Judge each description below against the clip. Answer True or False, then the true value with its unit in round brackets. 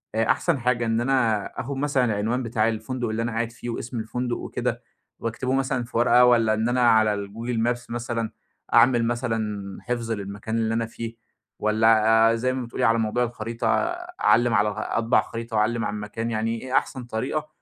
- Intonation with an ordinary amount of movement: False (1.7 semitones)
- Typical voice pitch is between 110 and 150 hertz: True (115 Hz)